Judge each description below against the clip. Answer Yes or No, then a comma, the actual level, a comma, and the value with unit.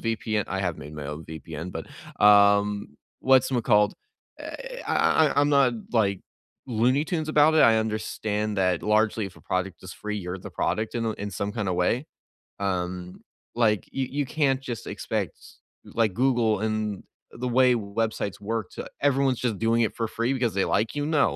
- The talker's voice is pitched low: Yes, low, 110 Hz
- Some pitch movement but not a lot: Yes, average, 4.1 semitones